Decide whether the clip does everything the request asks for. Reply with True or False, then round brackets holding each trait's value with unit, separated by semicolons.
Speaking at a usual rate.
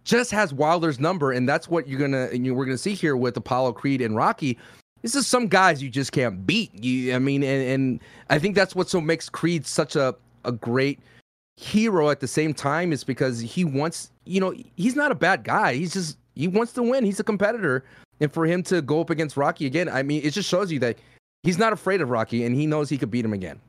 False (250 wpm)